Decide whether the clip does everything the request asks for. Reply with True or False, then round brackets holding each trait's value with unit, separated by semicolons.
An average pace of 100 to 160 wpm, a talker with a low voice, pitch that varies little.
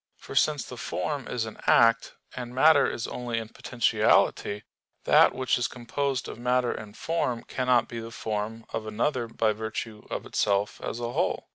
False (175 wpm; 115 Hz; 2.3 semitones)